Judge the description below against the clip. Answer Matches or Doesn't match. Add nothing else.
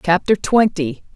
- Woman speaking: Matches